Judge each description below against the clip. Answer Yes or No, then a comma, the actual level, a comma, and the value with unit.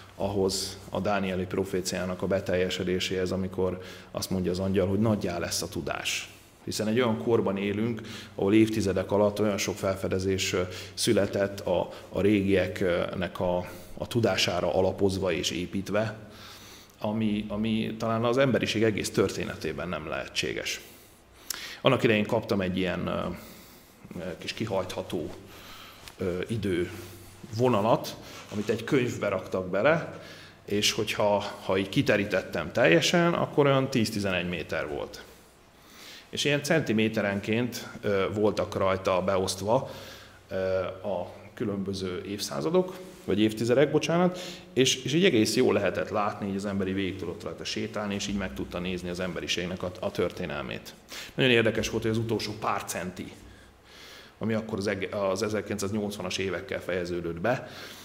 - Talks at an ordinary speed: Yes, average, 125 wpm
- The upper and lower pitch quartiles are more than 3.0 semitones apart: No, average, 2.7 semitones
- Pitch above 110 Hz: No, low, 100 Hz